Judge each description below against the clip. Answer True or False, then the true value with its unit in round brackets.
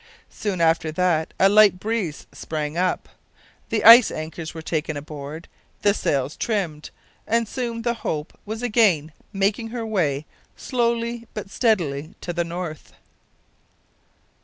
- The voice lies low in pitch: False (185 Hz)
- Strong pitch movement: True (6.2 semitones)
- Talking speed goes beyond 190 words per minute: False (135 wpm)